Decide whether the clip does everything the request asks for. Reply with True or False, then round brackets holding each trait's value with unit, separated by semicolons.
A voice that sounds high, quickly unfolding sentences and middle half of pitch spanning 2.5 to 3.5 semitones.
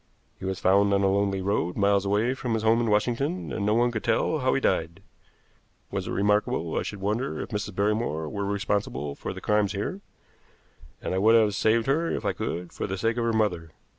False (105 Hz; 225 wpm; 2.8 semitones)